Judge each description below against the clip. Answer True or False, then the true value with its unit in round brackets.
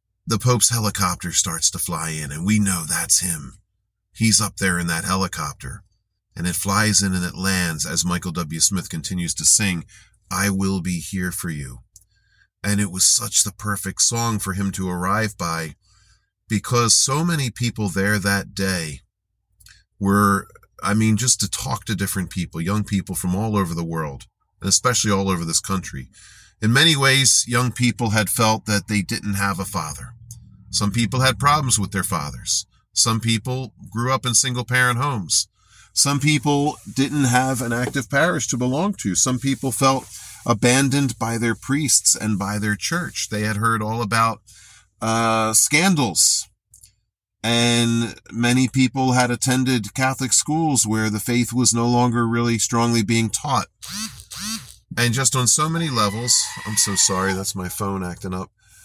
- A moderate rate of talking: True (170 wpm)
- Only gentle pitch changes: False (4.0 semitones)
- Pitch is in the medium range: False (110 Hz)